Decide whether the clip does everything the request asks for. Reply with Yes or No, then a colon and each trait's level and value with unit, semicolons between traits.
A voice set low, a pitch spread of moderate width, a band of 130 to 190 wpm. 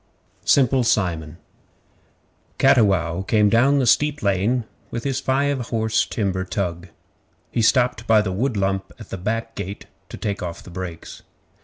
Yes: low, 110 Hz; average, 4.7 semitones; average, 150 wpm